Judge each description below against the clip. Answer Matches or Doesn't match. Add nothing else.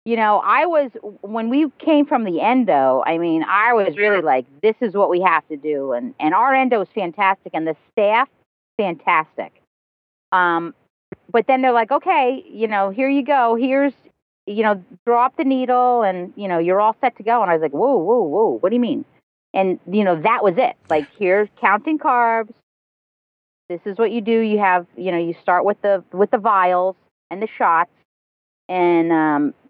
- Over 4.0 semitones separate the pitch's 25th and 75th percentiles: Matches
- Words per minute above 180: Matches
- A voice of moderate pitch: Doesn't match